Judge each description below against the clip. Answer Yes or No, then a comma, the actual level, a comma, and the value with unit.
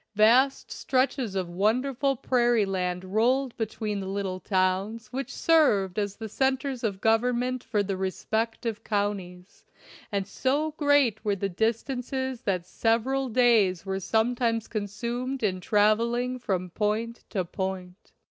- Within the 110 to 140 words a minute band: Yes, slow, 135 wpm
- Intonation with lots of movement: No, average, 4.3 semitones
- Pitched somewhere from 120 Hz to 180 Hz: No, high, 220 Hz